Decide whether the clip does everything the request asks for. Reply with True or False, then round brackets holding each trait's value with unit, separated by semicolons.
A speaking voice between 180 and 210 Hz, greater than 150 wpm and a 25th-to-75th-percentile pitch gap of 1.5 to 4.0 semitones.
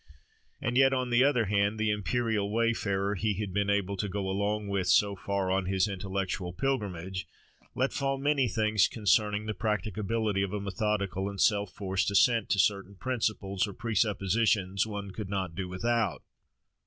False (100 Hz; 165 wpm; 2.4 semitones)